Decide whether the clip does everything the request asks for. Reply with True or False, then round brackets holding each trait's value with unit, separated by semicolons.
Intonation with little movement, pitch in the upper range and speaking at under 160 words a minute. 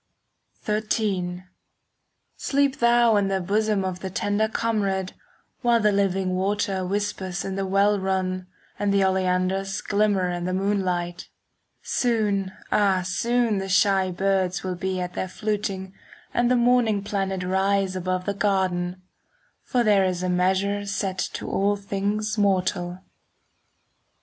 True (1.9 semitones; 195 Hz; 140 wpm)